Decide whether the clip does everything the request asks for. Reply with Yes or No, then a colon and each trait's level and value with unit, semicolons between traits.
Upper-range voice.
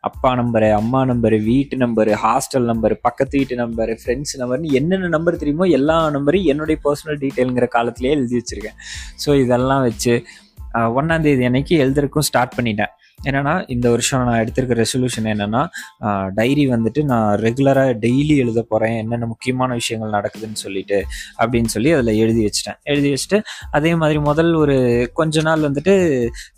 No: low, 125 Hz